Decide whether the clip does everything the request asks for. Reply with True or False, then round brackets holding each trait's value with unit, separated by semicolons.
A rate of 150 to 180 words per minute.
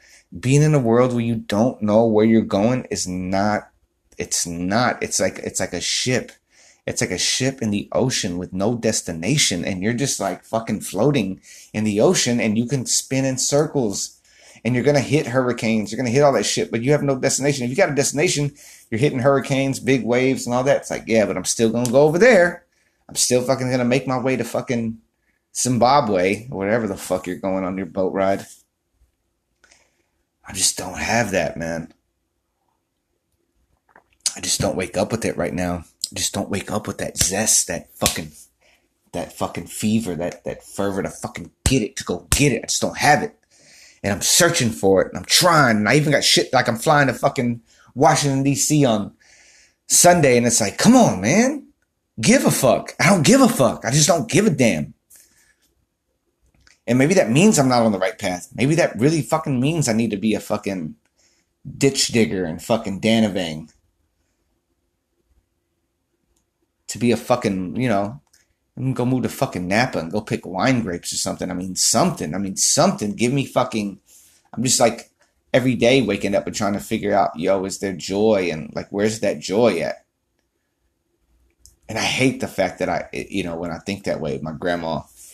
False (200 wpm)